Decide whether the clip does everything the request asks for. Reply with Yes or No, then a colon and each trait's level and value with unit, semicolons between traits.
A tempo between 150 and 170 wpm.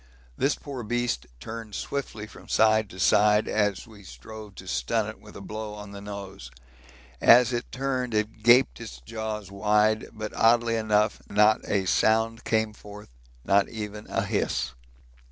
Yes: average, 160 wpm